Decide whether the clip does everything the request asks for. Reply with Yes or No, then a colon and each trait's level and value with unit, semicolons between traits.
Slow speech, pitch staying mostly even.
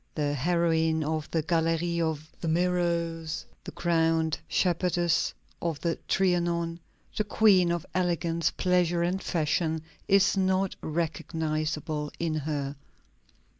Yes: slow, 115 wpm; narrow, 1.7 semitones